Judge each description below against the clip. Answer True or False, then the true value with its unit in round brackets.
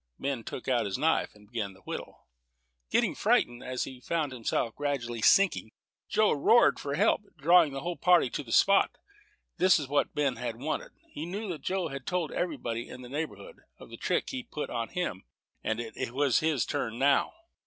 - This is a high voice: False (140 Hz)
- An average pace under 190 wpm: False (195 wpm)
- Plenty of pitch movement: True (5.9 semitones)